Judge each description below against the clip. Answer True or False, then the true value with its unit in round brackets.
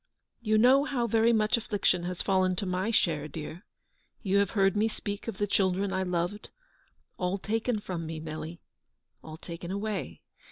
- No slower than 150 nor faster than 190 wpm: True (170 wpm)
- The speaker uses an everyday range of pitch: True (3.4 semitones)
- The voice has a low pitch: False (195 Hz)